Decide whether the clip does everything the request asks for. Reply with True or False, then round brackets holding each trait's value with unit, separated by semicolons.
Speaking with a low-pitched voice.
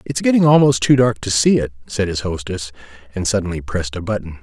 True (100 Hz)